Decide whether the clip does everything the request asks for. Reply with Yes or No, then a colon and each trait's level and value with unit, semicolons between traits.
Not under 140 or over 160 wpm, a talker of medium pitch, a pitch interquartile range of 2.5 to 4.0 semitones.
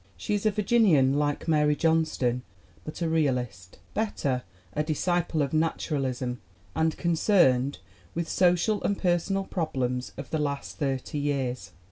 No: average, 145 wpm; medium, 150 Hz; average, 4.7 semitones